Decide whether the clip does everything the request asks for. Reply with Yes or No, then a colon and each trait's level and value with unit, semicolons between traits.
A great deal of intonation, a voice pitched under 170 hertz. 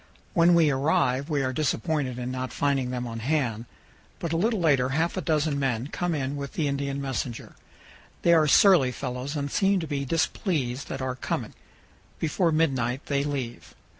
No: average, 3.7 semitones; medium, 140 Hz